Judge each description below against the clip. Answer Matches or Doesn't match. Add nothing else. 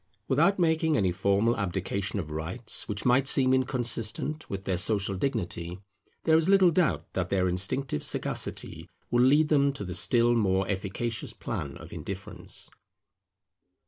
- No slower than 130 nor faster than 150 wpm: Matches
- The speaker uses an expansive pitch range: Matches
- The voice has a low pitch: Matches